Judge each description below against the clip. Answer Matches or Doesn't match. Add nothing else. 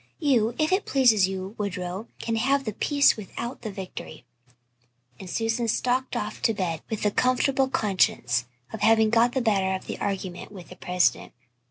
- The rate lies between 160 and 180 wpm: Matches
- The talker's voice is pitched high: Matches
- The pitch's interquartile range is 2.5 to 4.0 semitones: Doesn't match